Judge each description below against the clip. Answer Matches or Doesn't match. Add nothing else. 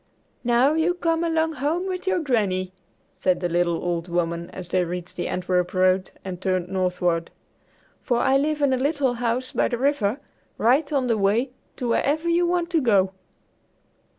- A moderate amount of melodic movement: Doesn't match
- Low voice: Doesn't match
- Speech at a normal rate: Matches